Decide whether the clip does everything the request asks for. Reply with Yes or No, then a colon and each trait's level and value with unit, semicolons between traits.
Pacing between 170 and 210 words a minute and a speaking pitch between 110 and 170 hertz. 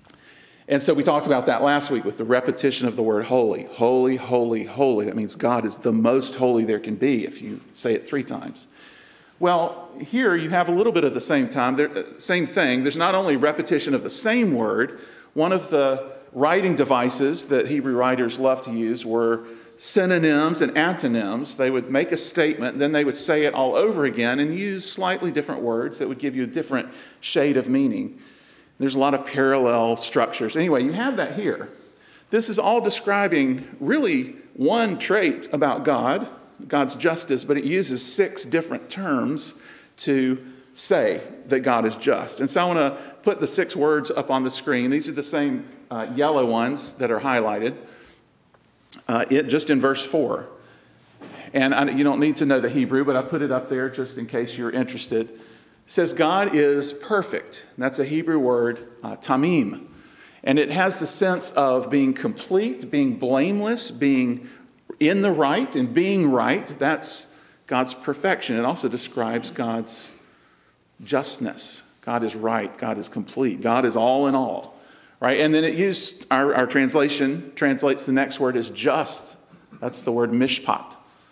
Yes: average, 180 wpm; medium, 140 Hz